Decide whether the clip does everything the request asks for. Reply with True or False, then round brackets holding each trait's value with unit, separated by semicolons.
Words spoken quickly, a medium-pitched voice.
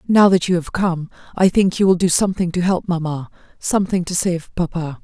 True (215 wpm; 175 Hz)